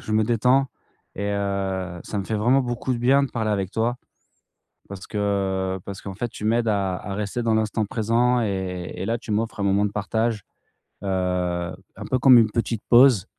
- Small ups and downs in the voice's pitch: No, average, 3.3 semitones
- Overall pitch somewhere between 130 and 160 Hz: No, low, 105 Hz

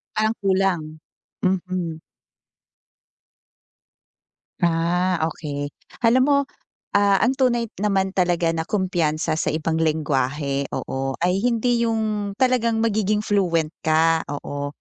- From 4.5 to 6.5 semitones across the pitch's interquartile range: Yes, average, 5.2 semitones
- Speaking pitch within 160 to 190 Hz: Yes, medium, 185 Hz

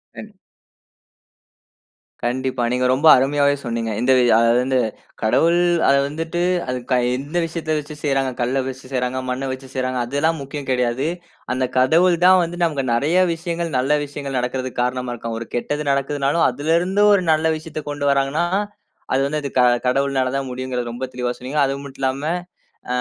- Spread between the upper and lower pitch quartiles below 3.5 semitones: Yes, average, 3.1 semitones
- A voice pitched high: No, low, 135 Hz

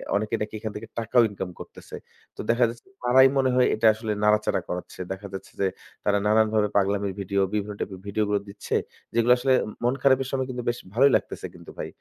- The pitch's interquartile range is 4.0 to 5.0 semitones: No, average, 3.2 semitones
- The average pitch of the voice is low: Yes, low, 110 Hz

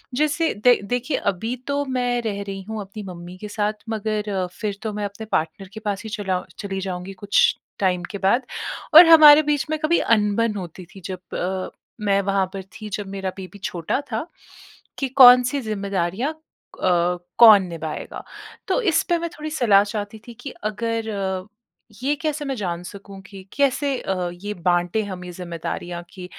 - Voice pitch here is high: Yes, high, 205 Hz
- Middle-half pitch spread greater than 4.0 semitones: Yes, average, 4.5 semitones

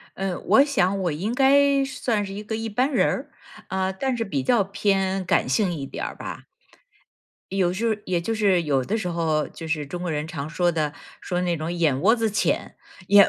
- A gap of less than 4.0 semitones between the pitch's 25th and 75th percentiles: No, average, 4.9 semitones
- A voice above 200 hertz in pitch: No, high, 190 Hz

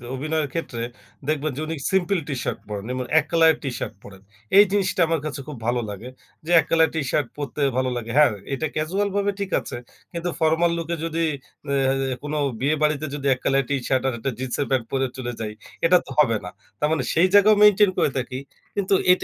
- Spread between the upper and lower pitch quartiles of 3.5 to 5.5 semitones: Yes, average, 4.4 semitones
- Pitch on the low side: No, medium, 150 Hz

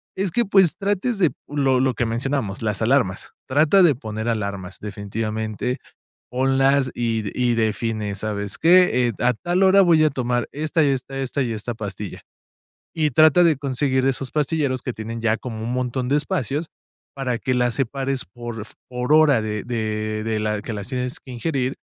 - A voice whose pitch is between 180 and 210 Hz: No, low, 125 Hz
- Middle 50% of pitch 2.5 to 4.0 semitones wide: No, average, 4.4 semitones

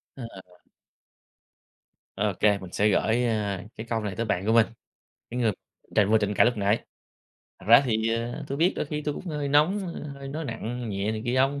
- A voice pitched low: Yes, low, 115 Hz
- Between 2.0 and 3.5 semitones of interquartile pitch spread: No, average, 4.5 semitones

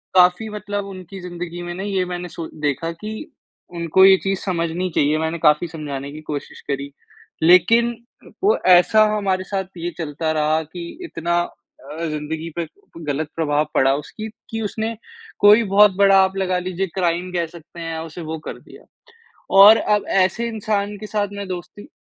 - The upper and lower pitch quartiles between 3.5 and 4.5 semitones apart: Yes, average, 3.8 semitones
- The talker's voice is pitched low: No, medium, 180 Hz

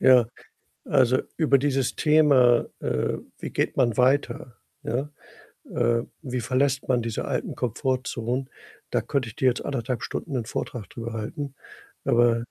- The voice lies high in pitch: No, low, 125 Hz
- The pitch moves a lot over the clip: No, narrow, 2.4 semitones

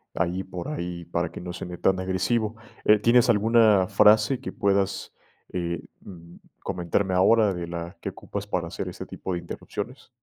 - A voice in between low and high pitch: No, very low, 95 Hz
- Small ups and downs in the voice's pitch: No, average, 3.4 semitones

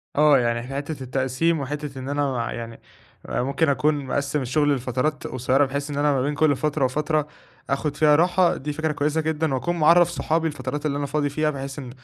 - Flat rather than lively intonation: Yes, narrow, 2.3 semitones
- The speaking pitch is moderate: Yes, medium, 145 Hz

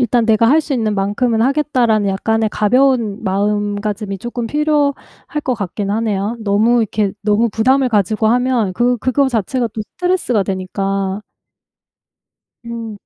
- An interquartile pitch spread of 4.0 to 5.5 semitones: No, average, 3.4 semitones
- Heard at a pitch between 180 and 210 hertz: No, high, 225 Hz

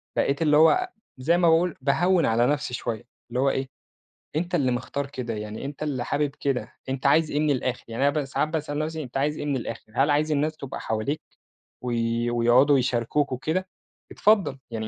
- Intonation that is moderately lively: Yes, average, 3.8 semitones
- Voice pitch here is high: No, medium, 140 Hz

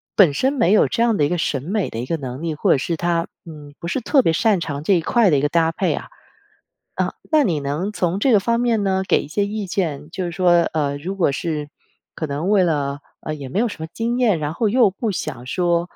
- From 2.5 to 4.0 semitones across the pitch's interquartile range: No, wide, 5.5 semitones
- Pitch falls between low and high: Yes, medium, 170 Hz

